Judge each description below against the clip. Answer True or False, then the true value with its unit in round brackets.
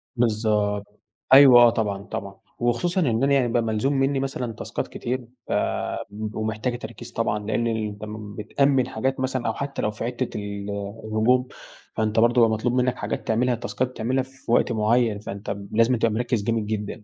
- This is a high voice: False (115 Hz)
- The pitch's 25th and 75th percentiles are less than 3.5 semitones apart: True (2.7 semitones)